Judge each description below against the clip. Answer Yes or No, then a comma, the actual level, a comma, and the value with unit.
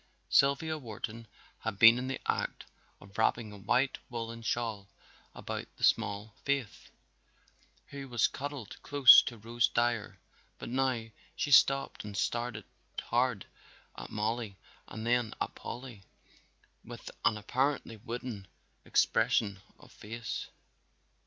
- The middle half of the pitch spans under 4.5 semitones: Yes, average, 3.1 semitones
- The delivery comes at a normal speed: No, slow, 125 wpm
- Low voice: Yes, low, 115 Hz